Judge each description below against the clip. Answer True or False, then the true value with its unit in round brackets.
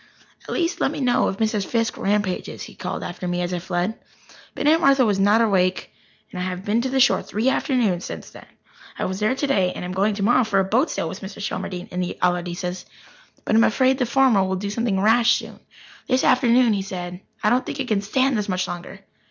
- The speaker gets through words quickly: True (235 wpm)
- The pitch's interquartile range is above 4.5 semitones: True (4.9 semitones)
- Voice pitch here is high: True (205 Hz)